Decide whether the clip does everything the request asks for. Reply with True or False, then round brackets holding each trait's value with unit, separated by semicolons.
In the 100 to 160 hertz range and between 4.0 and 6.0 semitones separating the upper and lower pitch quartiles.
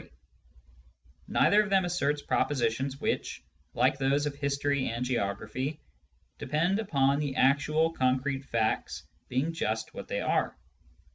False (140 Hz; 2.9 semitones)